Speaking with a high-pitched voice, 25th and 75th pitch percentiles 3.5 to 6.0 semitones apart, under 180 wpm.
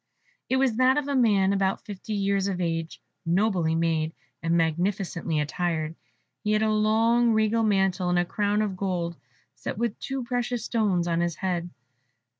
Yes: high, 195 Hz; average, 4.1 semitones; average, 165 wpm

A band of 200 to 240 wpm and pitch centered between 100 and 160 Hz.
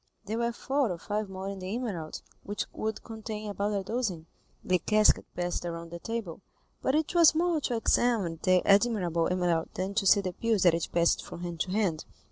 No: fast, 205 wpm; high, 200 Hz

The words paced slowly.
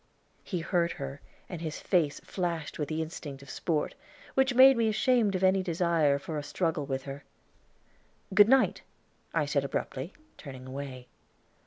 No: average, 160 wpm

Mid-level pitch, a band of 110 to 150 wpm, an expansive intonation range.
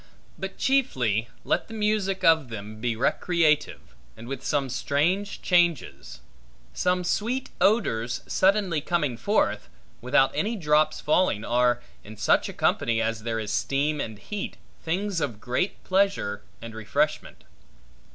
Yes: medium, 150 Hz; slow, 135 wpm; wide, 8.6 semitones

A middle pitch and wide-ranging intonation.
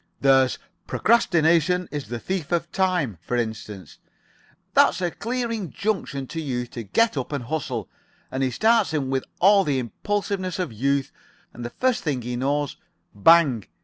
Yes: medium, 145 Hz; wide, 6.8 semitones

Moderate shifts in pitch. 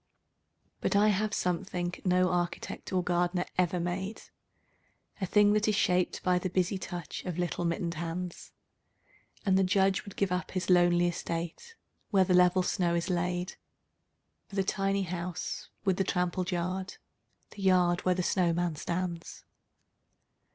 No: narrow, 1.5 semitones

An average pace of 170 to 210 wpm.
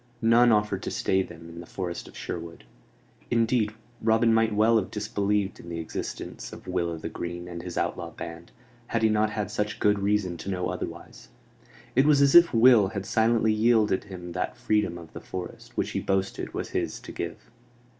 Yes: average, 195 wpm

